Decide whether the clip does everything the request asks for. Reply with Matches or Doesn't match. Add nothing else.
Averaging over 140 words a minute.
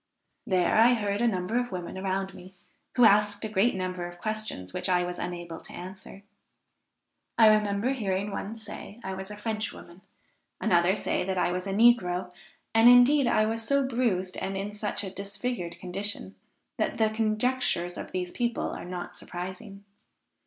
Matches